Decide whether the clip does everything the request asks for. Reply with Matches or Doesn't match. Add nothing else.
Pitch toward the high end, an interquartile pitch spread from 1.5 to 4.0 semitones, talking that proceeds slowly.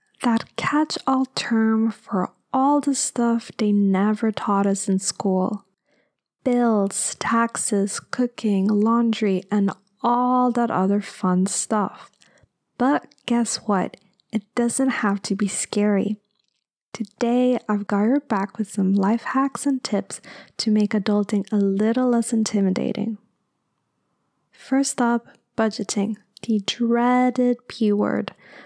Matches